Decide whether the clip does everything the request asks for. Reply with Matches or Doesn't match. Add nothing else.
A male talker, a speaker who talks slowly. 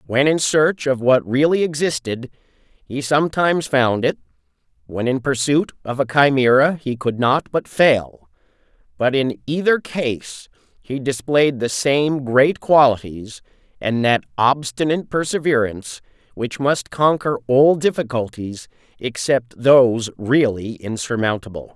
Matches